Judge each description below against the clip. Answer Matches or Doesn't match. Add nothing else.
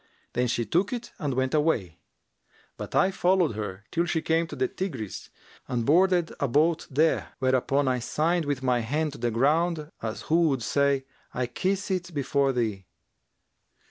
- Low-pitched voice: Doesn't match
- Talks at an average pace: Matches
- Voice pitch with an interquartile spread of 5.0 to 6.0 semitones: Matches